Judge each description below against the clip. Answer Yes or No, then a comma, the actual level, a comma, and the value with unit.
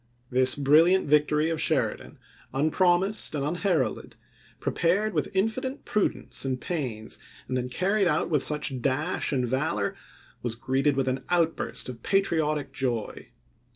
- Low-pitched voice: No, medium, 150 Hz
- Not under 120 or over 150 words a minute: Yes, average, 140 wpm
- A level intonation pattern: No, average, 5.2 semitones